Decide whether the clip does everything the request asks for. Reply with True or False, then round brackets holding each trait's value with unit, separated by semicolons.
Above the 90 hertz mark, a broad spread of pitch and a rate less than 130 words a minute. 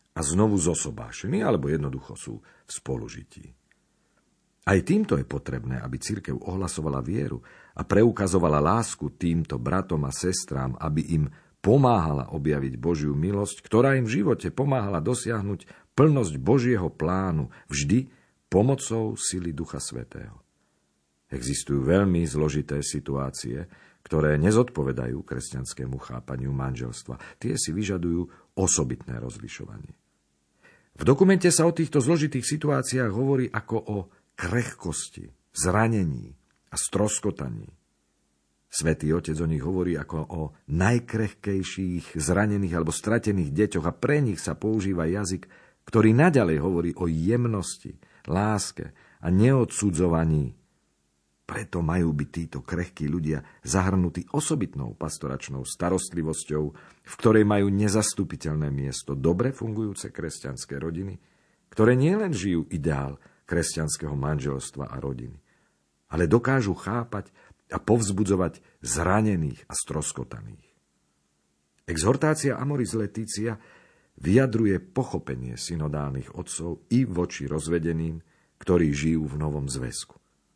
False (85 Hz; 6.5 semitones; 110 wpm)